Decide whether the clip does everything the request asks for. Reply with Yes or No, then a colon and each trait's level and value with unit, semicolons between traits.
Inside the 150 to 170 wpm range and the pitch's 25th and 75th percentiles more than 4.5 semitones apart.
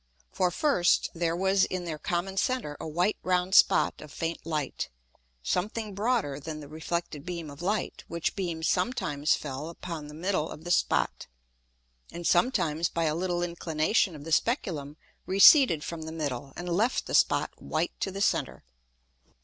No: average, 165 wpm; average, 3.5 semitones